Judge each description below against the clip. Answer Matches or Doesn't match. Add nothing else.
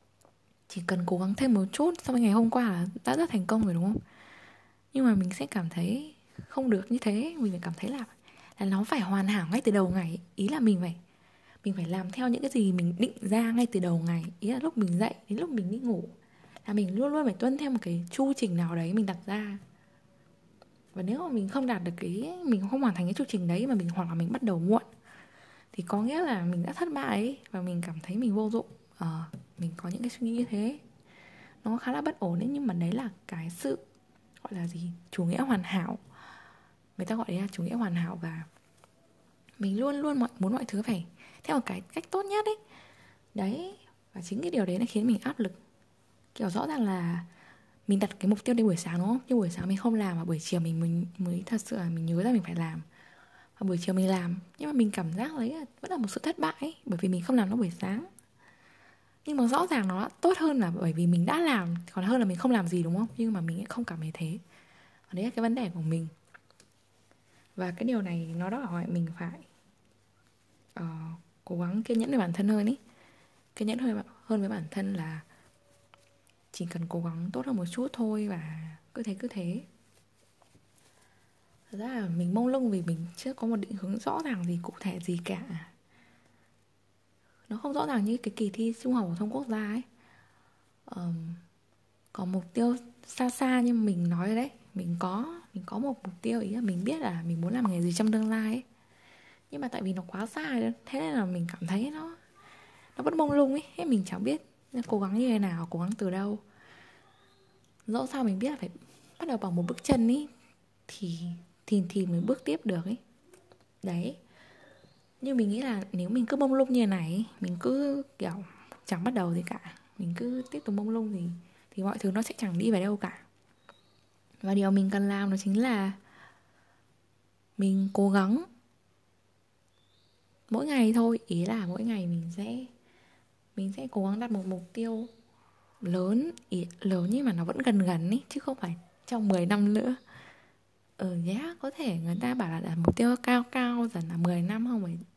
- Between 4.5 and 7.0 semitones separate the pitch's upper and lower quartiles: Matches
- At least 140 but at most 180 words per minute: Doesn't match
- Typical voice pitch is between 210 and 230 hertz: Doesn't match